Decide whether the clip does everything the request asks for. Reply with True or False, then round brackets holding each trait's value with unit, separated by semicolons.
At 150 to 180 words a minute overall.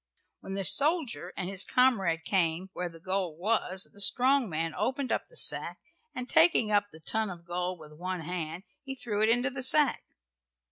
False (190 wpm)